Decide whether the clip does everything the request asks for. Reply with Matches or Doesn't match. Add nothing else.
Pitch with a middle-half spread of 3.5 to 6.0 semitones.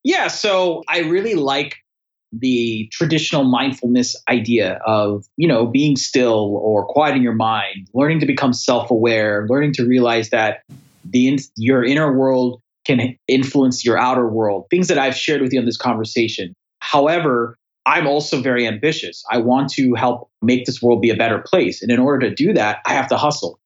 Doesn't match